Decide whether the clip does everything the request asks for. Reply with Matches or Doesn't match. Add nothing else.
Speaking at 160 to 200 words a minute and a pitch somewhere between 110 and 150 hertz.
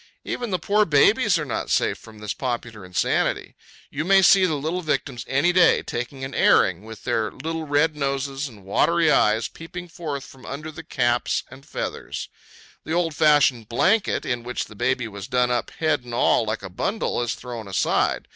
Matches